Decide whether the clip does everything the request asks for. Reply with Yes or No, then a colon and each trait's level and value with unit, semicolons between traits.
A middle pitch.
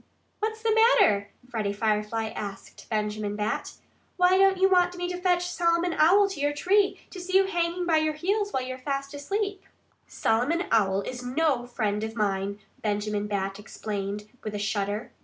No: very high, 265 Hz